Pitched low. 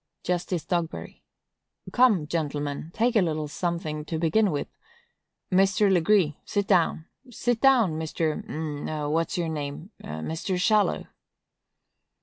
No: medium, 170 Hz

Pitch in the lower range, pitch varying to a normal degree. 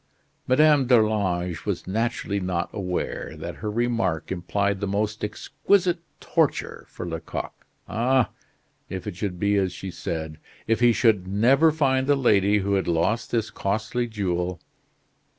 Yes: low, 105 Hz; average, 4.5 semitones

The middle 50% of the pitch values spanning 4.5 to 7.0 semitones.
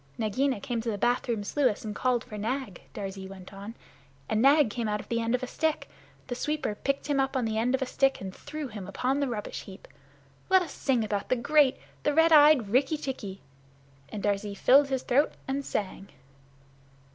Yes: average, 4.8 semitones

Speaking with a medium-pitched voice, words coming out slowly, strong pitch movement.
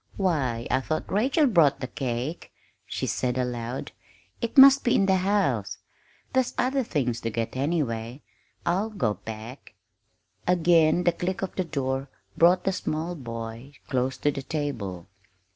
No: medium, 145 Hz; average, 150 wpm; wide, 6.9 semitones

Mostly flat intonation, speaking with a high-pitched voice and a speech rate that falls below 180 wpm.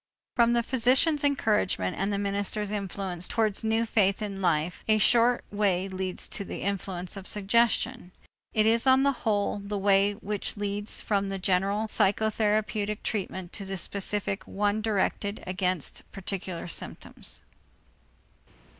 Yes: narrow, 2.1 semitones; high, 205 Hz; average, 140 wpm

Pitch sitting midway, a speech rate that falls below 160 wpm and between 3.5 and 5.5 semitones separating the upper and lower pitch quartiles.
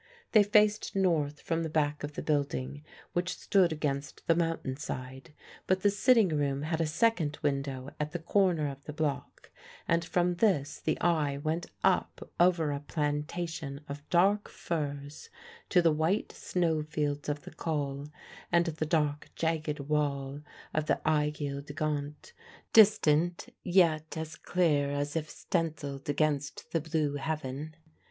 No: medium, 155 Hz; average, 150 wpm; average, 2.8 semitones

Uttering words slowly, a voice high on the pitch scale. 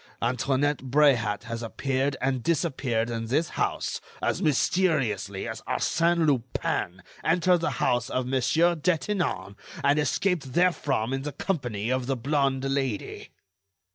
No: slow, 130 wpm; low, 135 Hz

